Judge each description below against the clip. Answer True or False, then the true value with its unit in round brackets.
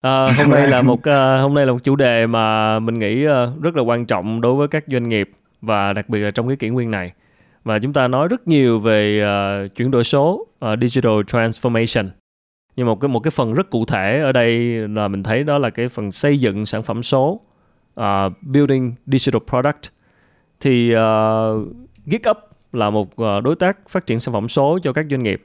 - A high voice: False (120 Hz)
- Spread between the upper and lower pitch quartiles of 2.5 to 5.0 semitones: True (3.9 semitones)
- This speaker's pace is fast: False (215 wpm)